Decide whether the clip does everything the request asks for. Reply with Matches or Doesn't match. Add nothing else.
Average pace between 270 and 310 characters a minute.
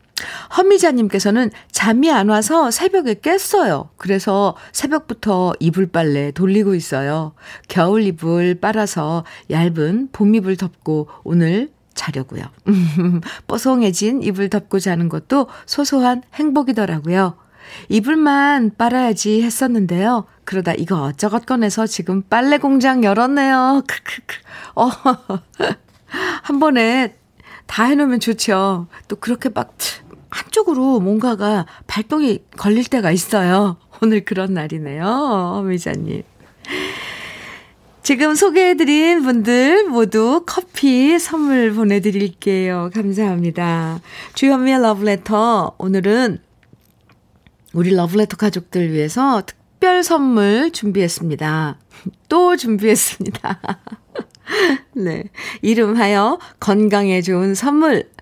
Doesn't match